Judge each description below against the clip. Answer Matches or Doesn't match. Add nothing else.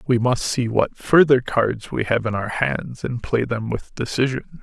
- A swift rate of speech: Matches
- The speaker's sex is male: Matches